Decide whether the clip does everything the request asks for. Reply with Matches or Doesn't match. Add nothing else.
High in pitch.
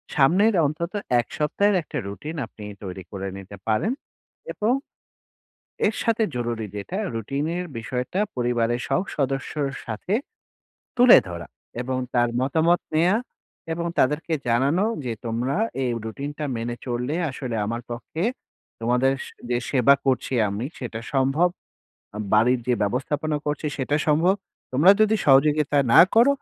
Doesn't match